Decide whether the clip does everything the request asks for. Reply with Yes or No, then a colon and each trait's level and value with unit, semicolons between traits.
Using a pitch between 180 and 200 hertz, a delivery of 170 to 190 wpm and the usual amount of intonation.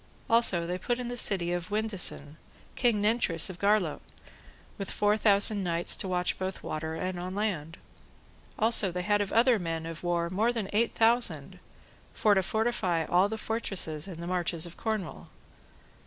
Yes: high, 190 Hz; average, 175 wpm; average, 4.0 semitones